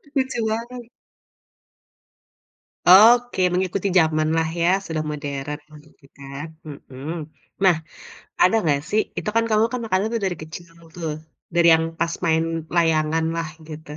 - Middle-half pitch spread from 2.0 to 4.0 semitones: No, average, 4.5 semitones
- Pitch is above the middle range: No, medium, 165 Hz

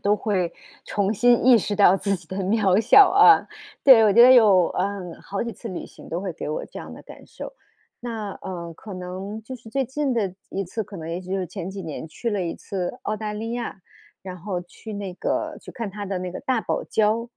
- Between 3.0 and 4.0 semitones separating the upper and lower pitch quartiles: Yes, average, 3.5 semitones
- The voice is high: Yes, high, 200 Hz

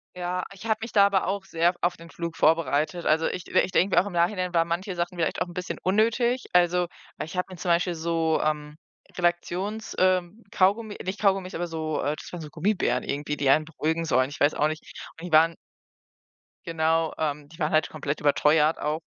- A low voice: No, medium, 170 Hz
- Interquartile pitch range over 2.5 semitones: Yes, average, 2.9 semitones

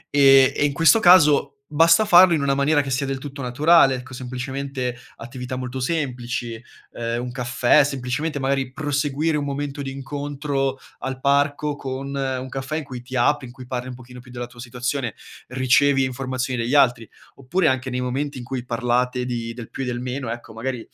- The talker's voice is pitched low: Yes, low, 130 Hz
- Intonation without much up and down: Yes, narrow, 2.2 semitones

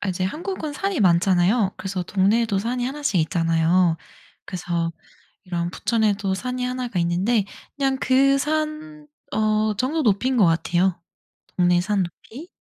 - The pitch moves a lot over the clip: Yes, wide, 6.3 semitones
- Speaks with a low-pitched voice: No, high, 210 Hz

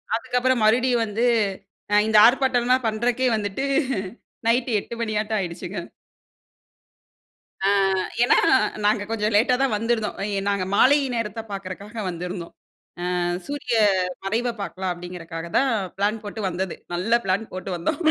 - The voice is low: No, high, 215 Hz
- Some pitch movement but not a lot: Yes, average, 3.8 semitones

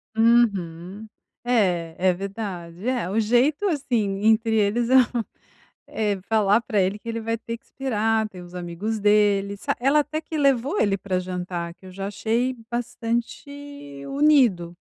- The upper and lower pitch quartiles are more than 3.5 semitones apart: Yes, average, 4.1 semitones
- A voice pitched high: Yes, high, 220 Hz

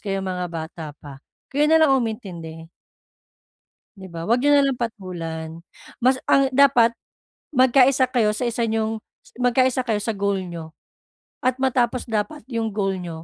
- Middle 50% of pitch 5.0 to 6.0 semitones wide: Yes, wide, 5.5 semitones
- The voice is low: No, high, 225 Hz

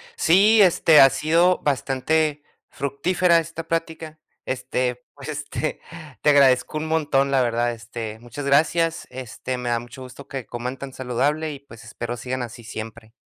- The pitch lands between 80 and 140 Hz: Yes, low, 135 Hz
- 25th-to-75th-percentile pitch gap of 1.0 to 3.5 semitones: No, average, 4.1 semitones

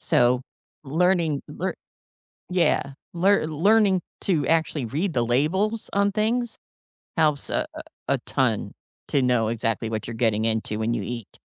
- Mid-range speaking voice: Yes, medium, 150 Hz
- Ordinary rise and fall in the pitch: No, wide, 8.1 semitones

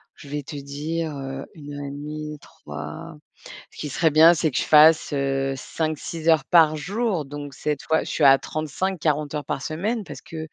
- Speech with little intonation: Yes, narrow, 2.1 semitones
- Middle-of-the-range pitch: Yes, medium, 150 Hz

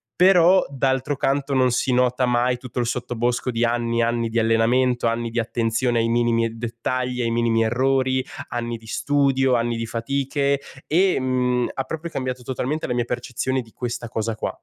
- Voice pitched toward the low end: Yes, low, 125 Hz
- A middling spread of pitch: No, narrow, 2.1 semitones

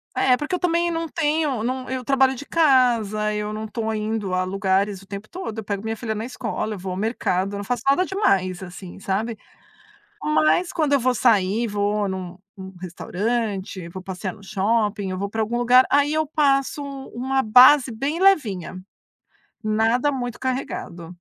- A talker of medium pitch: No, high, 225 Hz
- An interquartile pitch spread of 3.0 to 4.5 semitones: No, average, 5.2 semitones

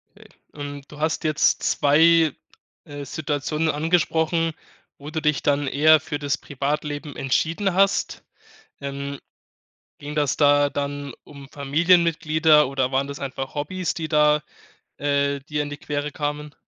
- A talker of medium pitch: Yes, medium, 145 Hz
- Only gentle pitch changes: Yes, narrow, 1.8 semitones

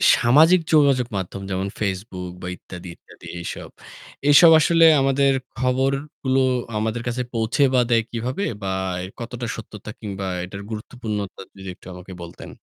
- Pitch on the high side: No, low, 115 Hz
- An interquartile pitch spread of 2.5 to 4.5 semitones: No, wide, 5.5 semitones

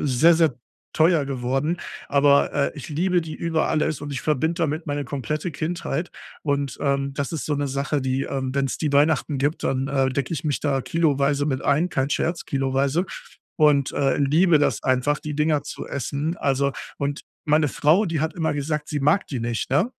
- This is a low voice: No, medium, 145 Hz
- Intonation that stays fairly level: Yes, narrow, 2.3 semitones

